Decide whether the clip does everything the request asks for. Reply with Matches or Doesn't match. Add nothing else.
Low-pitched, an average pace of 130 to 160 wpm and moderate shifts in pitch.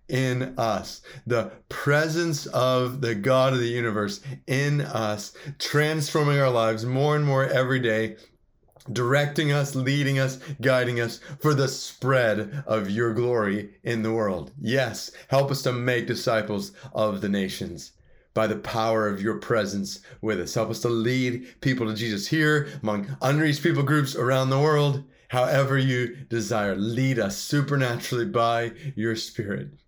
Matches